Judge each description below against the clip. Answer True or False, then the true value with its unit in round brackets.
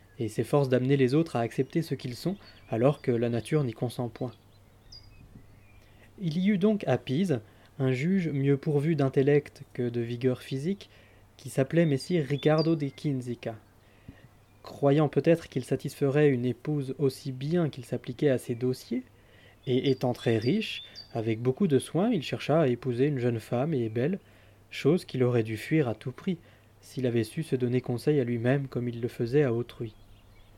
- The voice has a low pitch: True (125 Hz)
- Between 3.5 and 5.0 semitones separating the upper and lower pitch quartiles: True (4.0 semitones)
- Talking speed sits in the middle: True (175 wpm)